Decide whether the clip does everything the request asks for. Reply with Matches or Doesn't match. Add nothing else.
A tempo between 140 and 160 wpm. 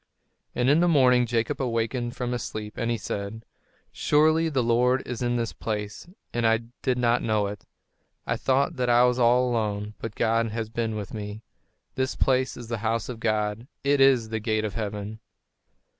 Doesn't match